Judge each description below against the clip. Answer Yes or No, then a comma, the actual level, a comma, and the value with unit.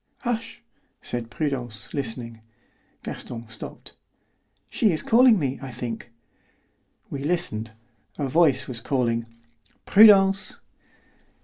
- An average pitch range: No, wide, 7.2 semitones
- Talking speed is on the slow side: Yes, slow, 100 wpm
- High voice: No, low, 135 Hz